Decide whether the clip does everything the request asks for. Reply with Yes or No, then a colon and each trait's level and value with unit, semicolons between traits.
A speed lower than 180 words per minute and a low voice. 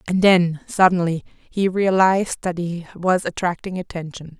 No: slow, 135 wpm; medium, 180 Hz